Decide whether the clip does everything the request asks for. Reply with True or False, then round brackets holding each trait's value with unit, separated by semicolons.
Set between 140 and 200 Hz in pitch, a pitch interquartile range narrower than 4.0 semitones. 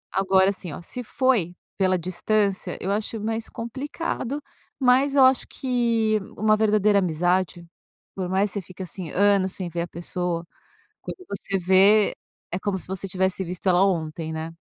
True (195 Hz; 3.3 semitones)